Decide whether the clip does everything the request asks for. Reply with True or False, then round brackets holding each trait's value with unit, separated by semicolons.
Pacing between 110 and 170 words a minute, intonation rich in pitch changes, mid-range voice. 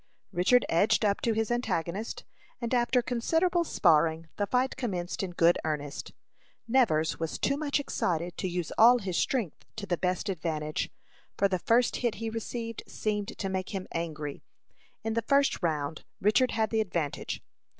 False (165 wpm; 5.8 semitones; 200 Hz)